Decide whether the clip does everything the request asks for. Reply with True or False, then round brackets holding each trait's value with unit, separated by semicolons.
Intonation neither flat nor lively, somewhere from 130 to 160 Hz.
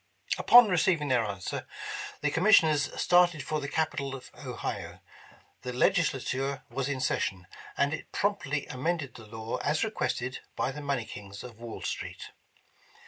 True (4.2 semitones; 140 Hz)